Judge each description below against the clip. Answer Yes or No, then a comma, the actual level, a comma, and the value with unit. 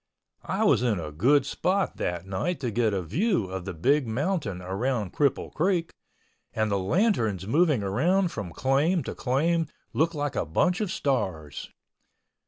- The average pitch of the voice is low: Yes, low, 130 Hz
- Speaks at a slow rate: No, average, 165 wpm